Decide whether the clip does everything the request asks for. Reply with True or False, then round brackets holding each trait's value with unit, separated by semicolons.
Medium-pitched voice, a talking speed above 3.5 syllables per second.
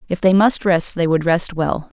True (175 Hz; 4.6 syllables/s)